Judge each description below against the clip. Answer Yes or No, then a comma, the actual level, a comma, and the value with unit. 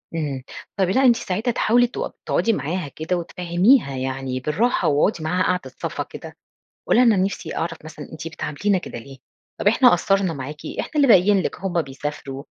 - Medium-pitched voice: Yes, medium, 175 Hz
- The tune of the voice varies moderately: No, wide, 5.7 semitones